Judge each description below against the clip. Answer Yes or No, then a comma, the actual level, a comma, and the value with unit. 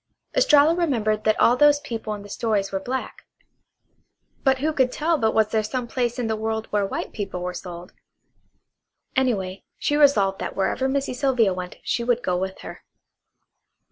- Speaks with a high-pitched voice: Yes, high, 225 Hz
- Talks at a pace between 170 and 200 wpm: Yes, average, 180 wpm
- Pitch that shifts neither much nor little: Yes, average, 4.9 semitones